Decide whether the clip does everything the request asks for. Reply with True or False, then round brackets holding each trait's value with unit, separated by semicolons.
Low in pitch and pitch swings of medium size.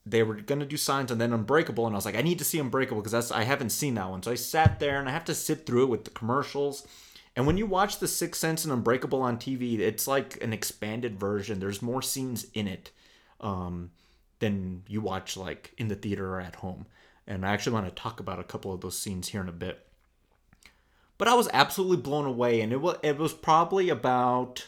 False (120 Hz; 6.0 semitones)